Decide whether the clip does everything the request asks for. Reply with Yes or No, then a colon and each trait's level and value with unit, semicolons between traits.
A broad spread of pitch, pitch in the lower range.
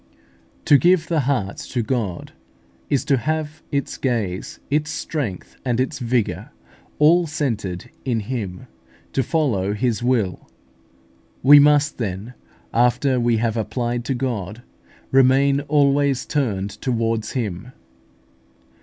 No: average, 4.2 semitones; low, 125 Hz